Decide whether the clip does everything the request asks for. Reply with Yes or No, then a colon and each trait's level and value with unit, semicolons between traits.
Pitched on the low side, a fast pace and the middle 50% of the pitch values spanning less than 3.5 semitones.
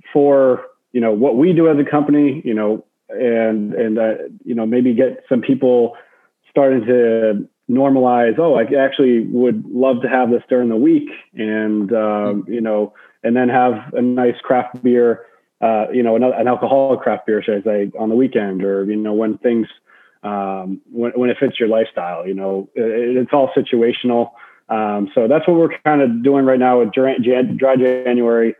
No: low, 120 Hz; average, 190 wpm; average, 2.9 semitones